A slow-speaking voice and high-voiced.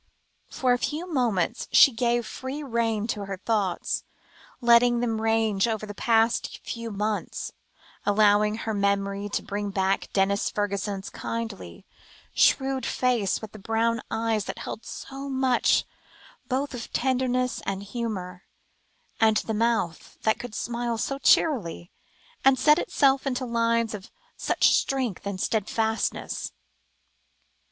Yes: slow, 130 wpm; high, 225 Hz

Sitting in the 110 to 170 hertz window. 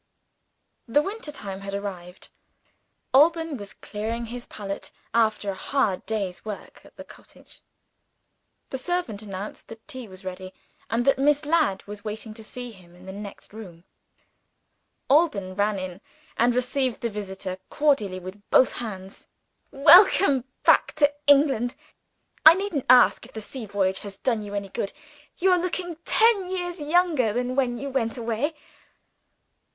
No: high, 230 Hz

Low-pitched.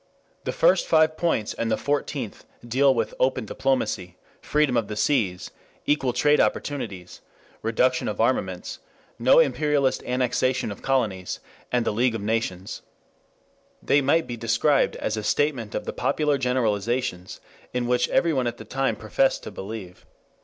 Yes: low, 125 Hz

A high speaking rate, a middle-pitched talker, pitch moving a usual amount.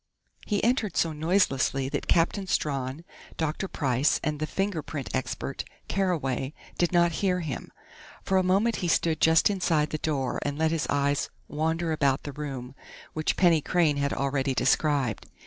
No: average, 160 wpm; medium, 155 Hz; average, 3.7 semitones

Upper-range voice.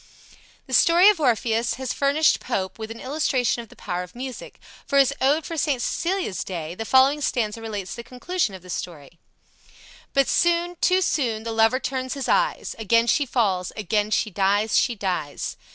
Yes: high, 235 Hz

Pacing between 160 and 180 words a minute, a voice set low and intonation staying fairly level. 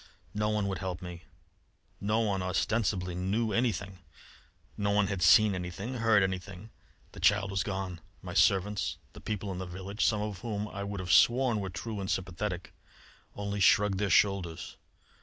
Yes: average, 170 wpm; low, 100 Hz; narrow, 2.3 semitones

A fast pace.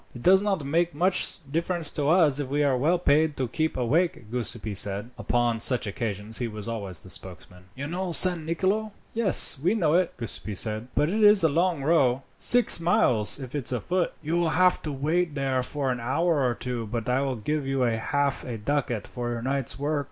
Yes: fast, 210 wpm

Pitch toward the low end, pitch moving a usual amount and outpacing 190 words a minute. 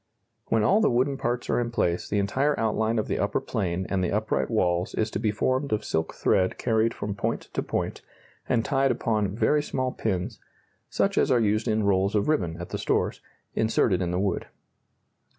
Yes: low, 110 Hz; average, 3.7 semitones; fast, 205 wpm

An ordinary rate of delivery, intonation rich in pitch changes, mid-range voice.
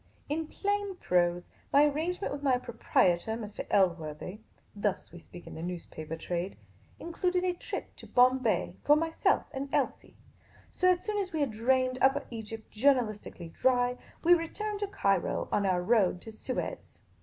No: average, 170 wpm; wide, 8.9 semitones; high, 245 Hz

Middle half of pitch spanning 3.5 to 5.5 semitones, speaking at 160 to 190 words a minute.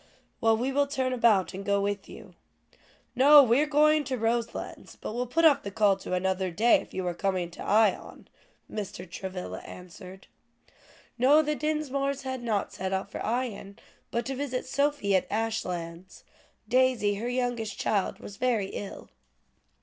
Yes: average, 5.1 semitones; average, 165 wpm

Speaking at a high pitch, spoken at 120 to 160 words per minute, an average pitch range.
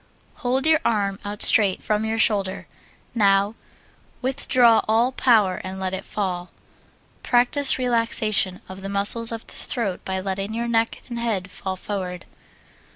Yes: high, 210 Hz; average, 150 wpm; average, 3.5 semitones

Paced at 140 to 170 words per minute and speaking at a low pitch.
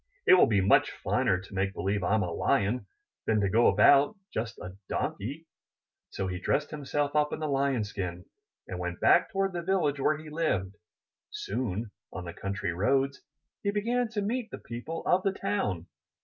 No: average, 185 wpm; low, 125 Hz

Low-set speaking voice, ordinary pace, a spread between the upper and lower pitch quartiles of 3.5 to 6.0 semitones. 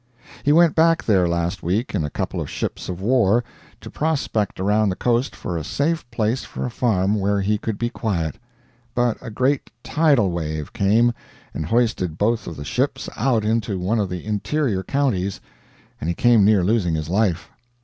Yes: low, 105 Hz; average, 190 wpm; average, 4.7 semitones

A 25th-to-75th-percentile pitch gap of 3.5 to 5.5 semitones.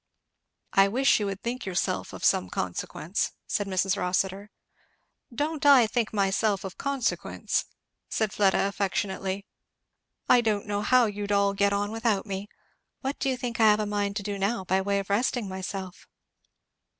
No: narrow, 2.6 semitones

